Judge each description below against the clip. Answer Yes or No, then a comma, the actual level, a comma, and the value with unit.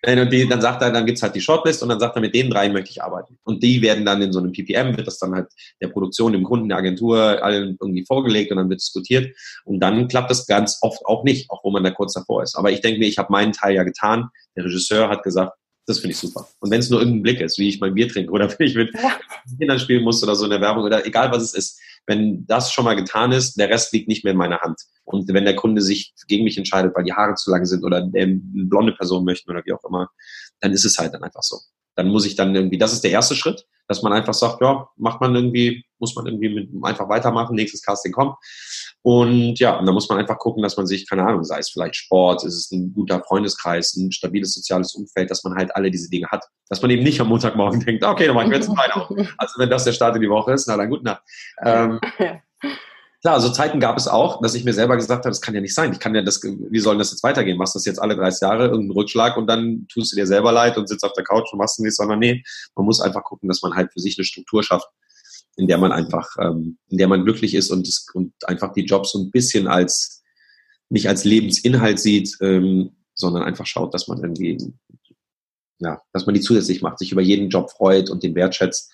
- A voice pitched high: No, low, 105 Hz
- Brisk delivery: Yes, fast, 260 wpm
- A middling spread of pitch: Yes, average, 3.6 semitones